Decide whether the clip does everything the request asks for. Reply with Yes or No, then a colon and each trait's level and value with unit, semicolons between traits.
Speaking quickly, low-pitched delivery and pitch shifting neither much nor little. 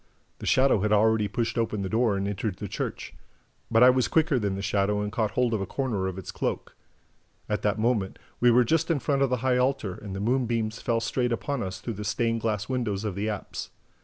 Yes: fast, 235 wpm; low, 115 Hz; average, 3.4 semitones